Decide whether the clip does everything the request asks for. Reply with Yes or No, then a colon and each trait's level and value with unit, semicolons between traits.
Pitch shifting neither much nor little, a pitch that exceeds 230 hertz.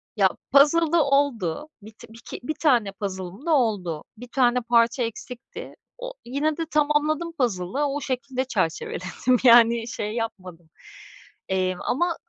No: wide, 5.9 semitones; high, 245 Hz